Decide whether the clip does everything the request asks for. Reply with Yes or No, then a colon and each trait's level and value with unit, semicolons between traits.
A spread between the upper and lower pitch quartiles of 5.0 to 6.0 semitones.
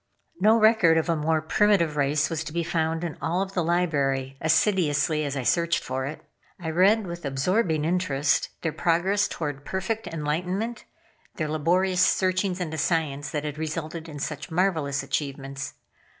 No: average, 3.5 semitones